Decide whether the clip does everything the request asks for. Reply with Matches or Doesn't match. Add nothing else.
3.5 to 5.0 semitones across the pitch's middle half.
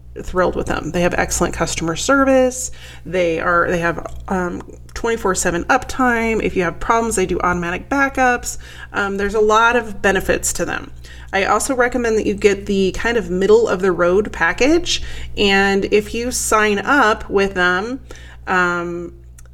Matches